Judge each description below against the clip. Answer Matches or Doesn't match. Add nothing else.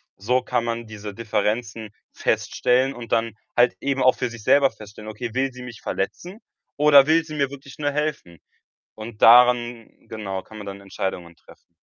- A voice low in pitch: Matches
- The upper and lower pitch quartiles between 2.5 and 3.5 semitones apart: Doesn't match